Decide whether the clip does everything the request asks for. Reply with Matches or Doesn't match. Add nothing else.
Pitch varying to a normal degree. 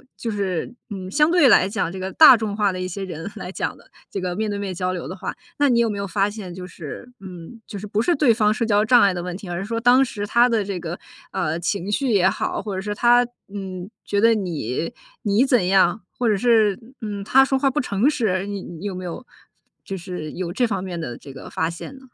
Matches